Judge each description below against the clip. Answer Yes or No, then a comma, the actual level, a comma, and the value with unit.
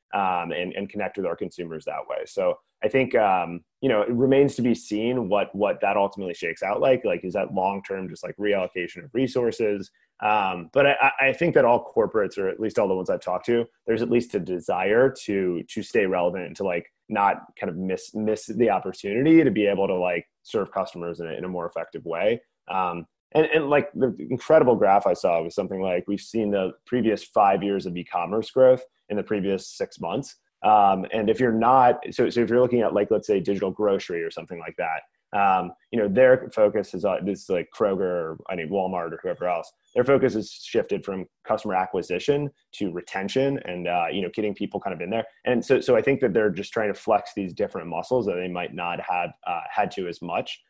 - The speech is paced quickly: Yes, fast, 230 wpm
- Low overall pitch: Yes, low, 110 Hz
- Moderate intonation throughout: No, wide, 5.9 semitones